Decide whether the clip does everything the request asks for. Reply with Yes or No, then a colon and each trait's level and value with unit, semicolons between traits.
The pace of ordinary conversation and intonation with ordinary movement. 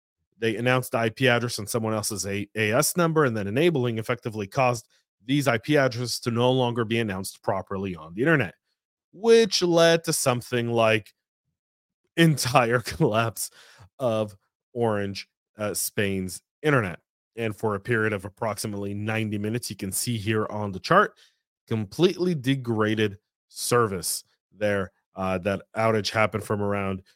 Yes: average, 145 wpm; average, 3.5 semitones